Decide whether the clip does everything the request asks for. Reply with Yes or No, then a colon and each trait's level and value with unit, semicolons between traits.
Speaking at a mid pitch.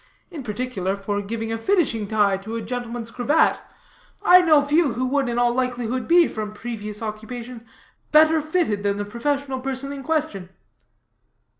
No: high, 240 Hz